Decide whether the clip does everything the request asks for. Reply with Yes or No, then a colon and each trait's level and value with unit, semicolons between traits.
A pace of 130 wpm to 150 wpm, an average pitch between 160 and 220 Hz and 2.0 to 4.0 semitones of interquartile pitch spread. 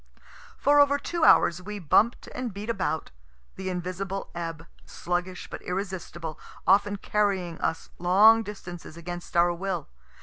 Yes: slow, 135 wpm; medium, 185 Hz; average, 2.9 semitones